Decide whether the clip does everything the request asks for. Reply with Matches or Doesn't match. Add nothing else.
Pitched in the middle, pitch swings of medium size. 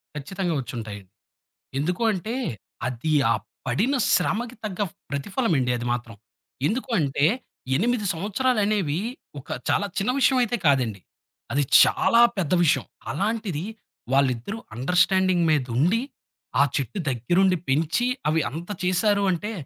Doesn't match